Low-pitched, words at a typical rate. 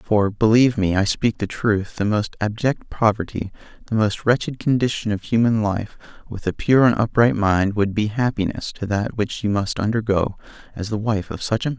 No: low, 110 Hz; fast, 215 wpm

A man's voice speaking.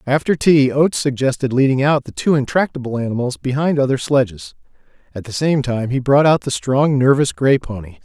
Yes: male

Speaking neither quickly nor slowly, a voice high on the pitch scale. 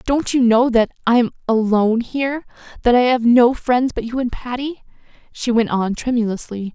Yes: average, 180 wpm; high, 240 Hz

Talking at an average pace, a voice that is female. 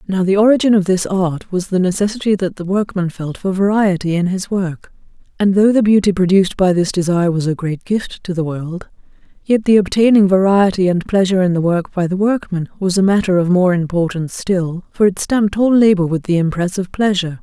No: fast, 215 wpm; female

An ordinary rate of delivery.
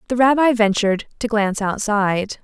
Yes: average, 150 wpm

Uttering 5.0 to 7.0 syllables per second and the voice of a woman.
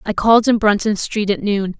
Yes: 5.5 syllables/s; female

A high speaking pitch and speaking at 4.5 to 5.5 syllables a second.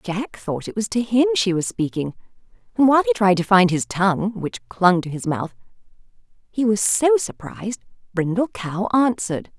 Yes: high, 210 Hz; 5.0 syllables/s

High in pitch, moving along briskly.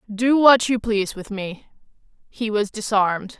No: high, 220 Hz; average, 160 wpm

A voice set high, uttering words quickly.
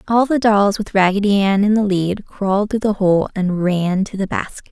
Yes: high, 200 Hz; fast, 230 wpm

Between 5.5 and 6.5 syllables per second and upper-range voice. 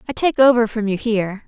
Yes: 6.1 syllables/s; high, 225 Hz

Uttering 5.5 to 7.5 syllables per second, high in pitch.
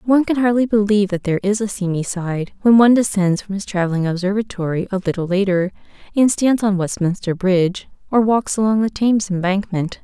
Yes: 5.9 syllables/s; high, 200 Hz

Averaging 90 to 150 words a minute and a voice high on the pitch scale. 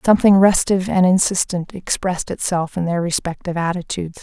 No: average, 140 wpm; medium, 180 Hz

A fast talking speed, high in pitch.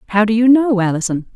Yes: fast, 220 wpm; high, 215 Hz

